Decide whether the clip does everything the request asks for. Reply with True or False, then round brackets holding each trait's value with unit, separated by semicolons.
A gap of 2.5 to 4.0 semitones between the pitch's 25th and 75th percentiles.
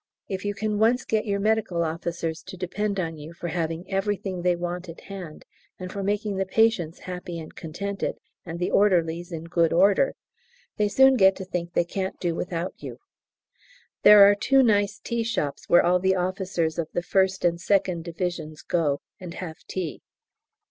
True (2.9 semitones)